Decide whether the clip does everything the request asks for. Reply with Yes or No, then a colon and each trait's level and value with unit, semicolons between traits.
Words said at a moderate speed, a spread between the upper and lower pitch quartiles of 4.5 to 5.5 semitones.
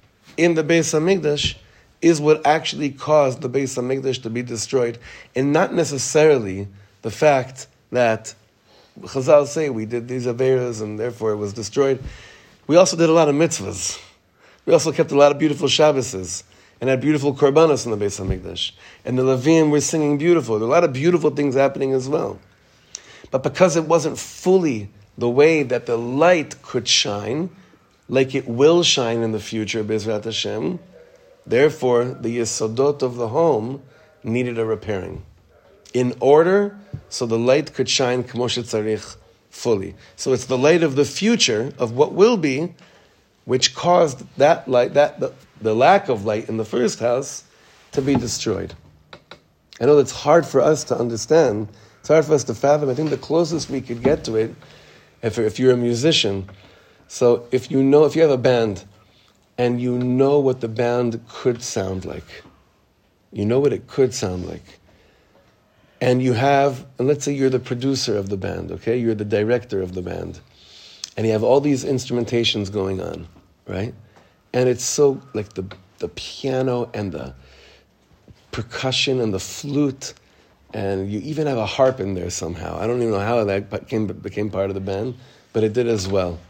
Yes: average, 180 wpm; average, 5.2 semitones